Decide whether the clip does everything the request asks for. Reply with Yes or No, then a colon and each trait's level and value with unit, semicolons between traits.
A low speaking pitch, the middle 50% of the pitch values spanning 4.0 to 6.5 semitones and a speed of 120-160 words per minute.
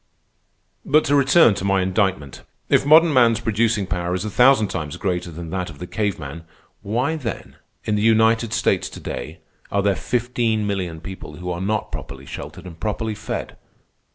No: low, 105 Hz; average, 4.3 semitones; average, 180 wpm